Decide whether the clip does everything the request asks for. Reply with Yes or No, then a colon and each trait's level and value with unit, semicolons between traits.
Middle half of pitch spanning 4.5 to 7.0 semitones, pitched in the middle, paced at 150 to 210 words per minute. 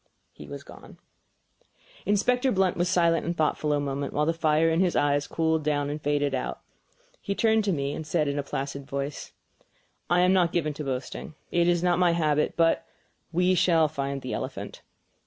No: average, 3.3 semitones; medium, 160 Hz; average, 195 wpm